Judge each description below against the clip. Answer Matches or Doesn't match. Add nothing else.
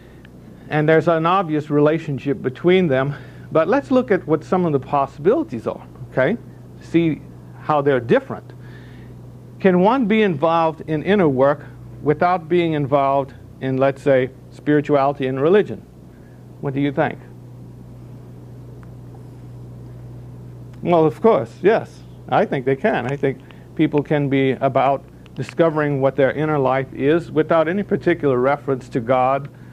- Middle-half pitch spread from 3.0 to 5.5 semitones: Matches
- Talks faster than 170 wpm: Doesn't match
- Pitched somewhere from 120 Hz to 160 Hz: Matches